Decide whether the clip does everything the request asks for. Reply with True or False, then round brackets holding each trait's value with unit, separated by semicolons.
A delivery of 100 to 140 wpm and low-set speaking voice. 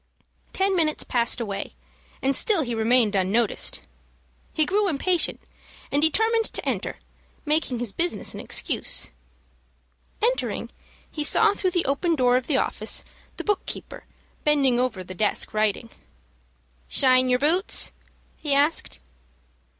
False (135 wpm; 280 Hz)